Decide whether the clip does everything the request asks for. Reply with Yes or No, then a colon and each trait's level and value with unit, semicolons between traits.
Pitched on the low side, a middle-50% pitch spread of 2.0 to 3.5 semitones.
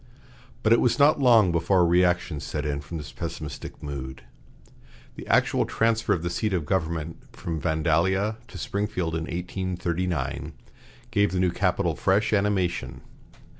No: very low, 90 Hz; average, 4.0 semitones